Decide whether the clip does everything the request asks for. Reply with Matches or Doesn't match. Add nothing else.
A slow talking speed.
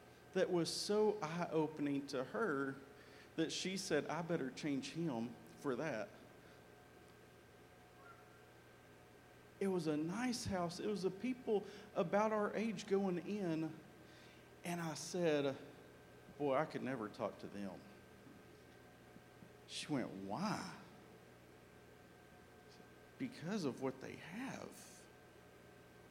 Matches